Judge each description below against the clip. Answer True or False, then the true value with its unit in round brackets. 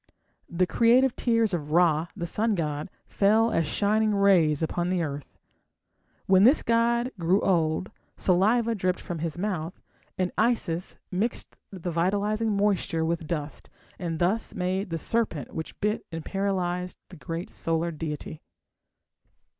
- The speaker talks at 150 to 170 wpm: False (140 wpm)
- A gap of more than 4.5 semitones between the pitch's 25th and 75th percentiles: False (4.2 semitones)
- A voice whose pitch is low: False (180 Hz)